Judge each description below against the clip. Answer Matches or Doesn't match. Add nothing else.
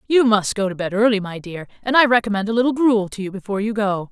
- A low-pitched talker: Doesn't match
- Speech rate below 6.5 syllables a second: Doesn't match